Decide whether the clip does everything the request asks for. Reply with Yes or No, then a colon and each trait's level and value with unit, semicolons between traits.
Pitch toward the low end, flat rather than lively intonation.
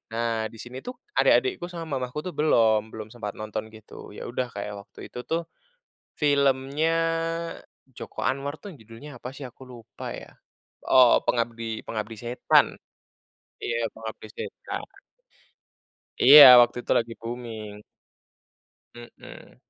No: low, 120 Hz; average, 3.9 semitones